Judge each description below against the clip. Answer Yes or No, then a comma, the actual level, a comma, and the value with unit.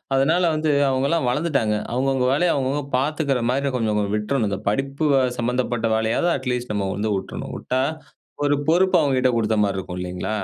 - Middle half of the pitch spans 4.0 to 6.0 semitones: Yes, average, 4.3 semitones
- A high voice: No, low, 130 Hz